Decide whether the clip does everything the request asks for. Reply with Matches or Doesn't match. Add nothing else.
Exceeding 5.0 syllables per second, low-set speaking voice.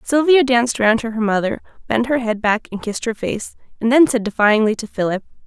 Doesn't match